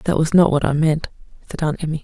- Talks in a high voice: No, medium, 155 Hz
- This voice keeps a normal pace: No, fast, 265 wpm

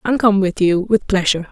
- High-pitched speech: Yes, high, 195 Hz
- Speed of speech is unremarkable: No, fast, 240 wpm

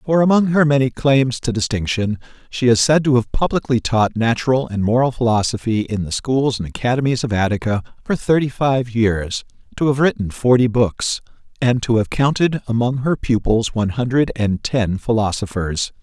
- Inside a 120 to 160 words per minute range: No, average, 170 wpm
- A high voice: No, low, 120 Hz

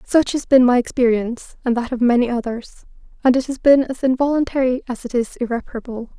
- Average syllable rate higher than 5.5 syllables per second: Yes, 6.0 syllables/s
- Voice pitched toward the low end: No, very high, 250 Hz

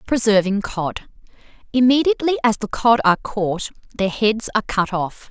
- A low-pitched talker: No, high, 215 Hz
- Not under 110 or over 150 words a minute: Yes, slow, 135 wpm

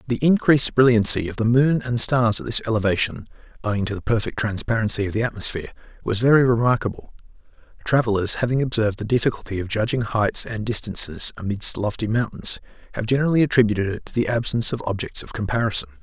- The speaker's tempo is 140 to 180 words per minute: Yes, average, 170 wpm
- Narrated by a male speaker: Yes, male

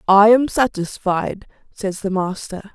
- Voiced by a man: No, female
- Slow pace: Yes, slow, 130 wpm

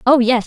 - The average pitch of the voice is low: No, high, 245 Hz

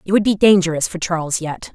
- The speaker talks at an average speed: No, fast, 240 wpm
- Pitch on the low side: No, medium, 180 Hz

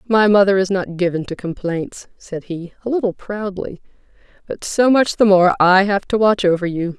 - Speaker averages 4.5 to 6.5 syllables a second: Yes, 4.9 syllables/s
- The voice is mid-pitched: No, high, 195 Hz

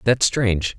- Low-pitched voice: Yes, low, 110 Hz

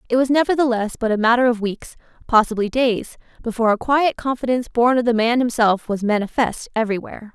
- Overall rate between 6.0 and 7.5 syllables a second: Yes, 6.2 syllables/s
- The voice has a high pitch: Yes, high, 235 Hz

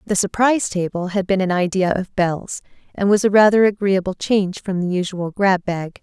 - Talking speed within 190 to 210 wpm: Yes, average, 200 wpm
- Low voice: No, high, 190 Hz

